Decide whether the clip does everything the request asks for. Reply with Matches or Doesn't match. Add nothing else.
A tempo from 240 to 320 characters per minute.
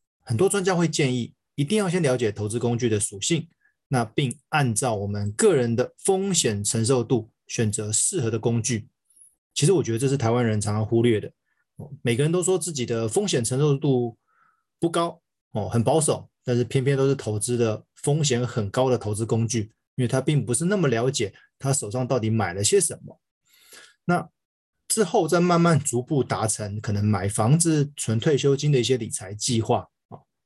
Matches